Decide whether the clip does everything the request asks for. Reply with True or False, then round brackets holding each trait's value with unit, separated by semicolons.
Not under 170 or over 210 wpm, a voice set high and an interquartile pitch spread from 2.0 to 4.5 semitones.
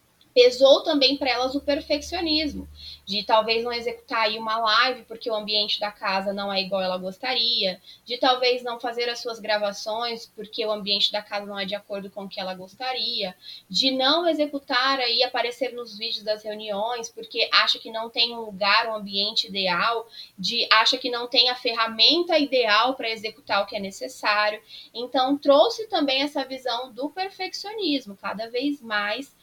True (180 wpm; 230 Hz; 4.0 semitones)